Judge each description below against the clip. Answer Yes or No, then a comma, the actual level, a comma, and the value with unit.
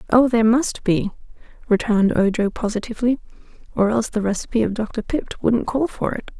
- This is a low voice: No, high, 225 Hz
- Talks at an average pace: Yes, average, 170 wpm